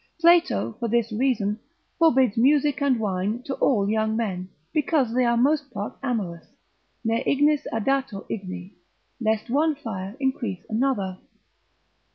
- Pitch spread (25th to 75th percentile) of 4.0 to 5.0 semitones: Yes, average, 4.7 semitones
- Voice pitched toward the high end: Yes, high, 235 Hz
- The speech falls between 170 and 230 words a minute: No, slow, 135 wpm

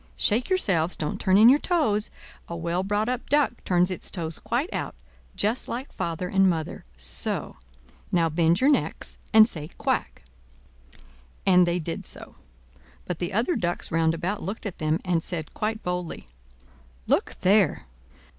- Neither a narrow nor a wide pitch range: Yes, average, 4.6 semitones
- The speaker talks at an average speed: Yes, average, 155 wpm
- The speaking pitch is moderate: Yes, medium, 180 Hz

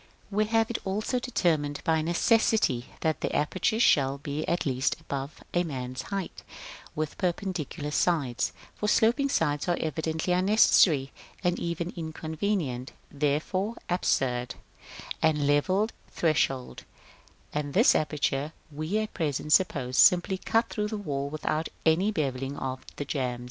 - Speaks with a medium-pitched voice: Yes, medium, 160 Hz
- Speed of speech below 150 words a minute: Yes, average, 140 wpm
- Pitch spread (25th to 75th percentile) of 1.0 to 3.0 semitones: No, average, 5.1 semitones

